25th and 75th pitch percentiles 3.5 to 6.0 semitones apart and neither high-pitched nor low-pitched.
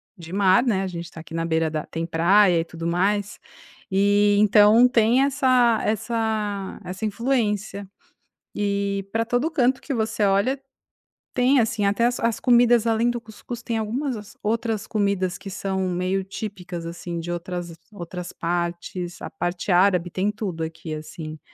No: average, 4.3 semitones; high, 200 Hz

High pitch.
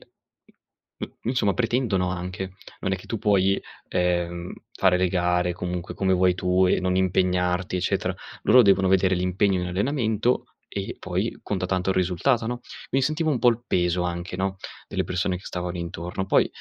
No: very low, 95 Hz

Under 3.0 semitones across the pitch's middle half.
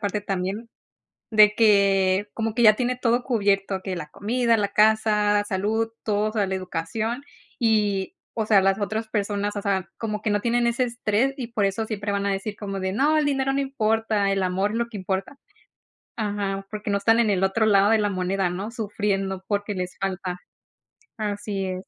Yes: narrow, 2.4 semitones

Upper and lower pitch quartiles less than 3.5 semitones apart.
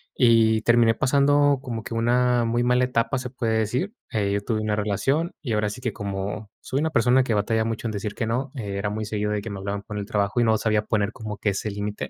Yes: average, 2.9 semitones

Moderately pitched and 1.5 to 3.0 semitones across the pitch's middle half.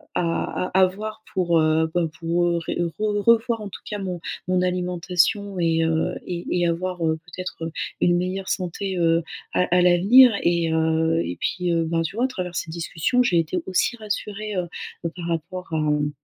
Yes: medium, 175 Hz; narrow, 2.4 semitones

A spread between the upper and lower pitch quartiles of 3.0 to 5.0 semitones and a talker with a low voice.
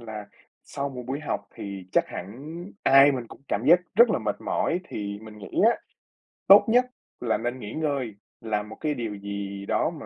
No: wide, 5.6 semitones; low, 115 Hz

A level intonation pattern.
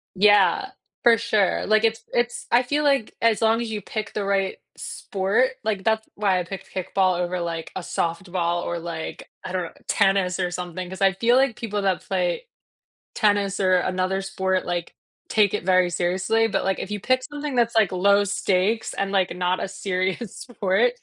No: average, 3.3 semitones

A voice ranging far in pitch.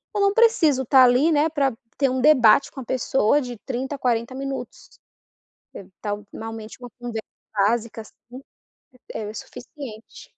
No: average, 3.7 semitones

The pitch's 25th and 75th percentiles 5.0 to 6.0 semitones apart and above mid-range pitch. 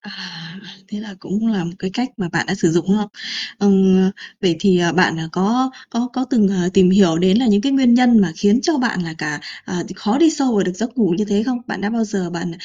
No: average, 4.2 semitones; high, 200 Hz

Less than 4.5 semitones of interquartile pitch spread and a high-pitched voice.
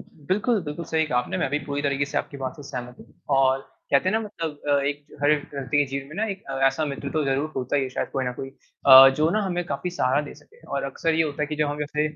No: average, 2.7 semitones; medium, 145 Hz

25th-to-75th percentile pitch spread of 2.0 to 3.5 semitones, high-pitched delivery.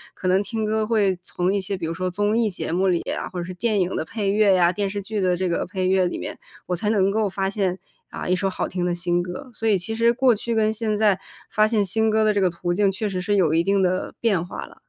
Yes: average, 2.9 semitones; high, 195 Hz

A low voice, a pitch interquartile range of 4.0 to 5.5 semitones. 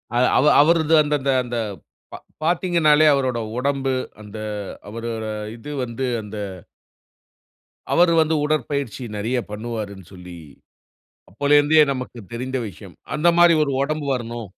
Yes: low, 130 Hz; average, 4.7 semitones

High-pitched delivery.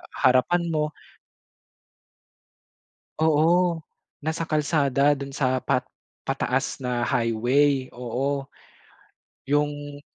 No: medium, 145 Hz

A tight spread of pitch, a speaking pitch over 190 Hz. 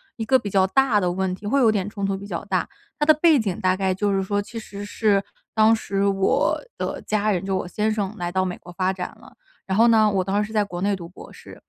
Yes: narrow, 2.3 semitones; high, 200 Hz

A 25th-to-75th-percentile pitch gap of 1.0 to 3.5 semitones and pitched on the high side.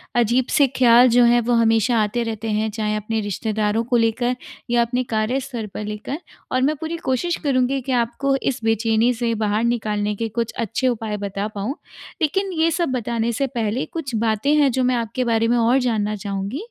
Yes: average, 2.8 semitones; high, 235 Hz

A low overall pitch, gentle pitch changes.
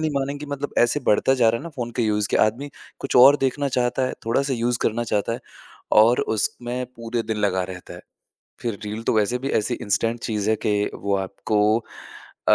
No: low, 115 Hz; average, 3.3 semitones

